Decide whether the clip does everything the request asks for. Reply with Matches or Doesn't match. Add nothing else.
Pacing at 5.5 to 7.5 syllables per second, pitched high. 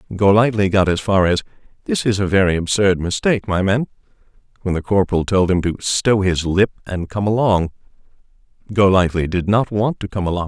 Doesn't match